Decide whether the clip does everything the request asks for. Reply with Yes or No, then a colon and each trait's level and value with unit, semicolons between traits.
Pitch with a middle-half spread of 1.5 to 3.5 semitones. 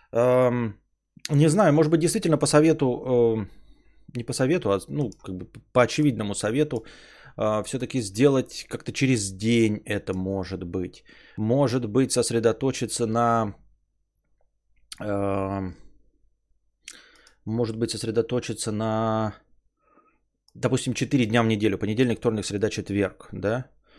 No: average, 4.0 semitones